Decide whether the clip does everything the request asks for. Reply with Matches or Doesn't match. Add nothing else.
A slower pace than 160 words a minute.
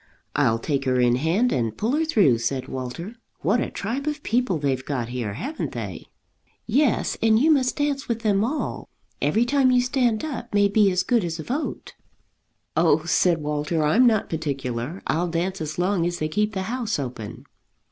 Doesn't match